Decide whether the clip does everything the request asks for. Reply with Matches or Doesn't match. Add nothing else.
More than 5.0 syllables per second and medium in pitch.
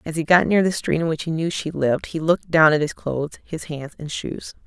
Matches